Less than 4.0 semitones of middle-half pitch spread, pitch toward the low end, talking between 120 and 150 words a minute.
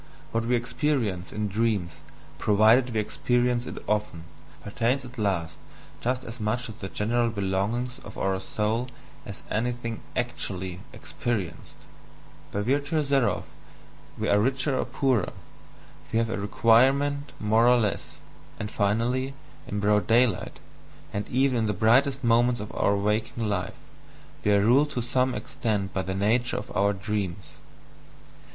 Yes: average, 3.4 semitones; low, 115 Hz; average, 145 wpm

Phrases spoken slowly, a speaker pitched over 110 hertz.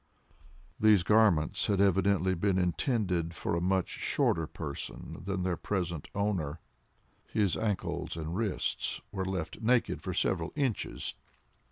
No: slow, 130 wpm; very low, 95 Hz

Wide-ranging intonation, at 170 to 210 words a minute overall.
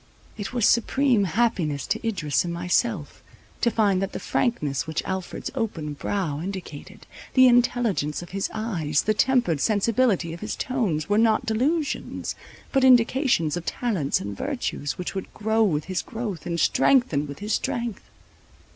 No: wide, 6.1 semitones; average, 155 wpm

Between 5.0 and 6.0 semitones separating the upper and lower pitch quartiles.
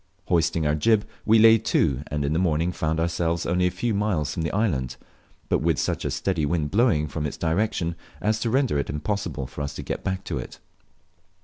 Yes: wide, 5.5 semitones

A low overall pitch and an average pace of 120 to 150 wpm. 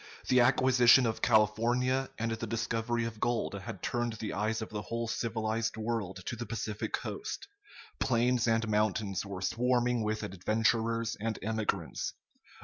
Yes: low, 115 Hz; average, 145 wpm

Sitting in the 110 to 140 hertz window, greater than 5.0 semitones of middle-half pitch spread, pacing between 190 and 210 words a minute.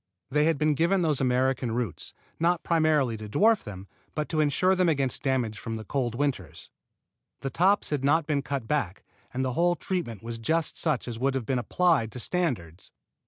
Yes: low, 135 Hz; wide, 5.5 semitones; average, 195 wpm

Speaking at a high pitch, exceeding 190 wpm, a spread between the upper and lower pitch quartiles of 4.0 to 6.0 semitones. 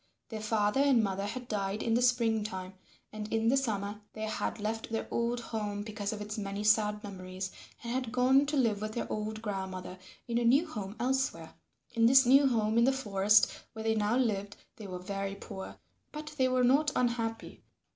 No: high, 220 Hz; average, 200 wpm; average, 3.0 semitones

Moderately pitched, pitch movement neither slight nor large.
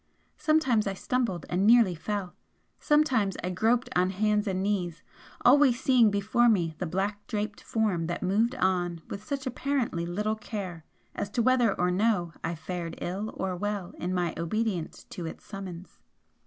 No: high, 200 Hz; average, 4.1 semitones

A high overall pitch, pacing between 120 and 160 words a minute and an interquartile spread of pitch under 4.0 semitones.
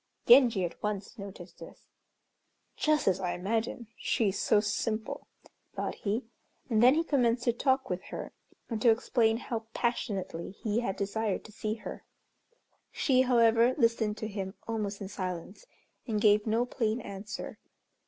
Yes: high, 220 Hz; average, 155 wpm; average, 2.9 semitones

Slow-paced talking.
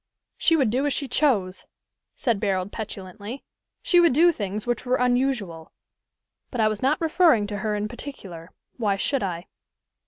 No: average, 165 wpm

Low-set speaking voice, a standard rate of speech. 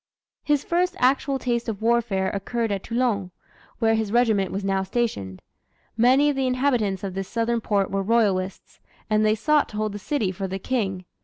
No: high, 220 Hz; average, 185 wpm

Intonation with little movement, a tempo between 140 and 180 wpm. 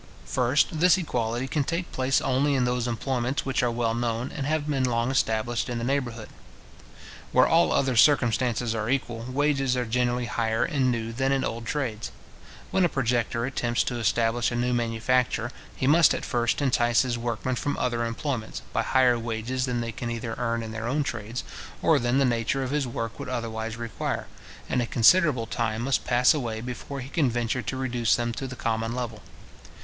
No: narrow, 2.3 semitones; average, 195 wpm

